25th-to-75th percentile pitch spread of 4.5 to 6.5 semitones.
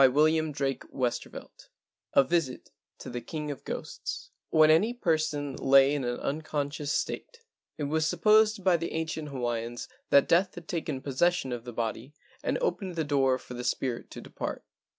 No: average, 3.8 semitones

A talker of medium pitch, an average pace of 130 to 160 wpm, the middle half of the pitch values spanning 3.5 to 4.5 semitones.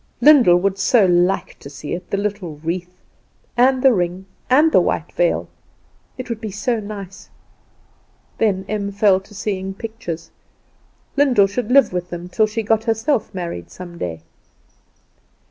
No: high, 200 Hz; average, 155 wpm; average, 4.1 semitones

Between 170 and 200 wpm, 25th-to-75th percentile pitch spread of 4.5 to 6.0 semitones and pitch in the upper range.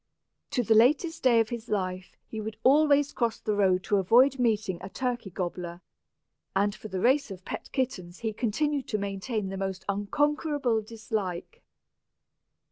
No: average, 160 wpm; average, 4.9 semitones; high, 220 Hz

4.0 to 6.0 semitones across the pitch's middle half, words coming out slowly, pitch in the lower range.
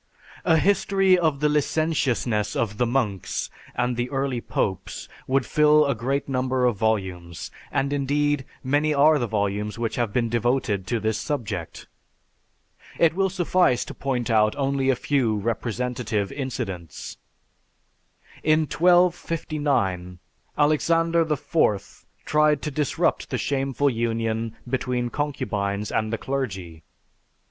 Yes: average, 5.2 semitones; slow, 125 wpm; low, 125 Hz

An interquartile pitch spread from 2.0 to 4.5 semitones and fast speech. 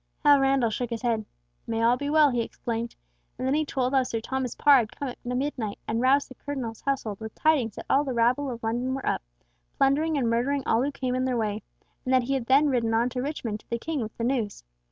Yes: average, 3.0 semitones; fast, 250 wpm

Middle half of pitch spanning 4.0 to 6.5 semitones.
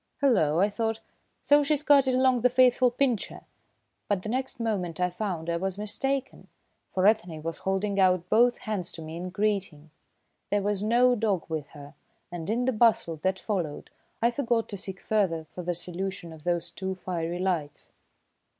Yes: average, 5.1 semitones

